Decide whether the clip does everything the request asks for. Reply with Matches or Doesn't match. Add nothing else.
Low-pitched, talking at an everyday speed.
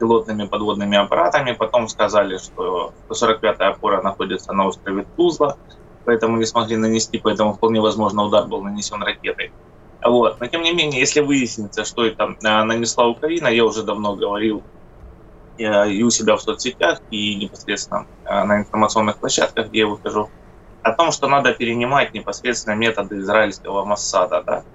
Matches